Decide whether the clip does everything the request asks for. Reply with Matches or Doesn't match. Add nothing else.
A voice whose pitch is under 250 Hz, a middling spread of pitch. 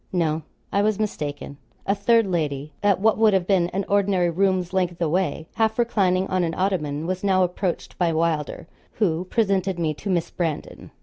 Matches